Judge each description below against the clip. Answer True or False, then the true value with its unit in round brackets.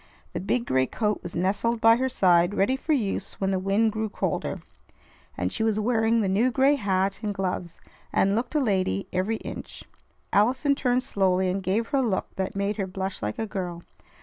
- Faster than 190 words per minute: True (200 wpm)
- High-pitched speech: True (205 Hz)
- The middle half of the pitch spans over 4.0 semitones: False (3.6 semitones)